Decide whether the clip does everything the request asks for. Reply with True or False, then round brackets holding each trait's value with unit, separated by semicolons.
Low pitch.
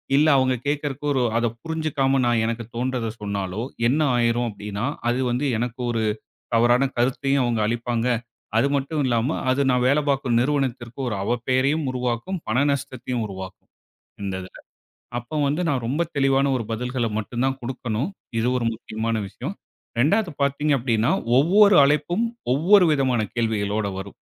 True (125 Hz)